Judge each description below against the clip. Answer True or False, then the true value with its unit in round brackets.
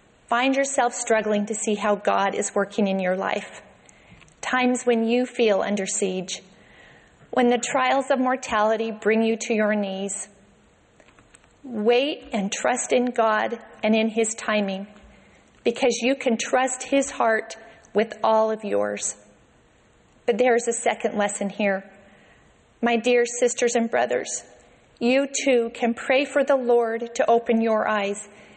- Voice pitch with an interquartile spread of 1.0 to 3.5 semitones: True (2.8 semitones)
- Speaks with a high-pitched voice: True (225 Hz)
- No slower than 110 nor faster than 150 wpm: True (145 wpm)